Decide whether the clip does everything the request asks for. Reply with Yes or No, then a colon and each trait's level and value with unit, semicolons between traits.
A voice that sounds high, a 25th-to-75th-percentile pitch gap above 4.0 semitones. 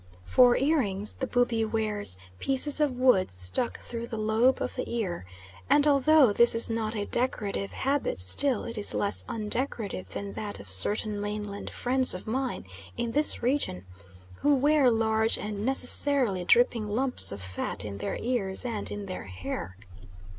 Yes: high, 225 Hz; average, 4.4 semitones